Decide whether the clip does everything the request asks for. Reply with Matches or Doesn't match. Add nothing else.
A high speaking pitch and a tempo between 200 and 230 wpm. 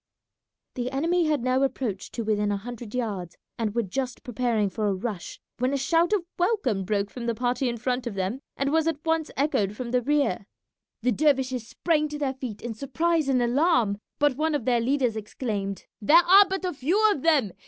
Matches